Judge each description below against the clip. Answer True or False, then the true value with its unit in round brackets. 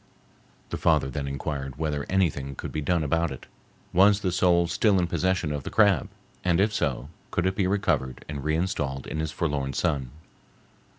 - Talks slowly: False (185 wpm)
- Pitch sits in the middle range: False (80 Hz)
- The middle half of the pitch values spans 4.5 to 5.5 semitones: True (4.9 semitones)